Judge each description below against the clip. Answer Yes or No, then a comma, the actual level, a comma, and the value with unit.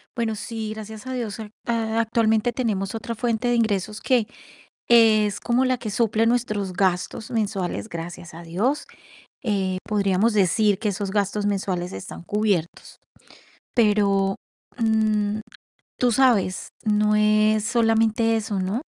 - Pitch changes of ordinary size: No, narrow, 2.3 semitones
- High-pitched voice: Yes, high, 215 Hz